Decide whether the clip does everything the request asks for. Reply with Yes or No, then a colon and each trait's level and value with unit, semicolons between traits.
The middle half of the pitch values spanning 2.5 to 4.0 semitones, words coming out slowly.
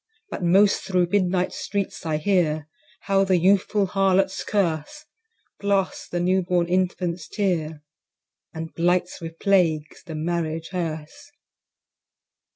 Yes: average, 2.9 semitones; slow, 120 wpm